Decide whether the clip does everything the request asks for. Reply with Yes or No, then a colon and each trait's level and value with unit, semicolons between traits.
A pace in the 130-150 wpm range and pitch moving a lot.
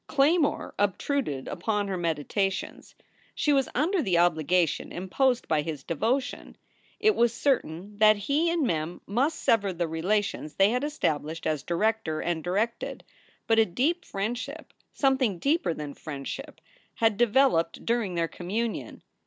Yes: average, 140 wpm; wide, 7.7 semitones